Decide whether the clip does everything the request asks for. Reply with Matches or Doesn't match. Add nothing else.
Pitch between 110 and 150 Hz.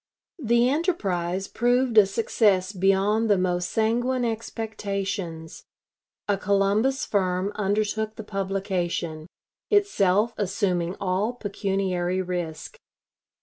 Doesn't match